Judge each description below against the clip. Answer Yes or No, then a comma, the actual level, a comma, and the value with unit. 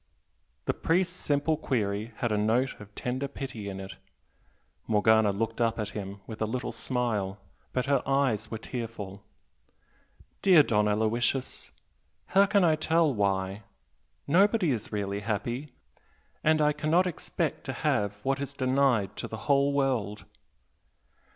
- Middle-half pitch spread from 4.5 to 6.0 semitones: Yes, average, 5.2 semitones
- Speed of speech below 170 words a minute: Yes, average, 145 wpm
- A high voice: No, low, 120 Hz